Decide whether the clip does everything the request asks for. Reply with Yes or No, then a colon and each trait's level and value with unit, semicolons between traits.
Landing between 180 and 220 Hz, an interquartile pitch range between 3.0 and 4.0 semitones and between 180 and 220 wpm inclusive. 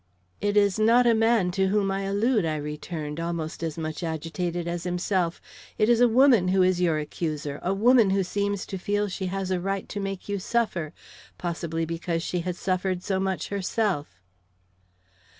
Yes: medium, 185 Hz; average, 3.3 semitones; average, 185 wpm